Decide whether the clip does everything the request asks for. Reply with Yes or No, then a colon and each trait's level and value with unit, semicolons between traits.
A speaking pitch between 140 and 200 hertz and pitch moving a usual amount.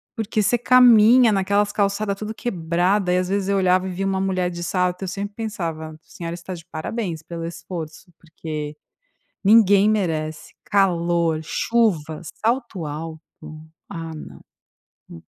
Yes: medium, 185 Hz; average, 3.7 semitones